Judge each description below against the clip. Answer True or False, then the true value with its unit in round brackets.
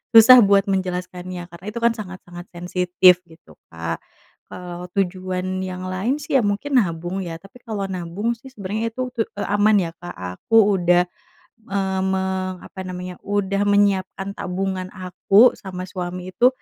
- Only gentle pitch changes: True (2.2 semitones)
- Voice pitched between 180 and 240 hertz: True (190 Hz)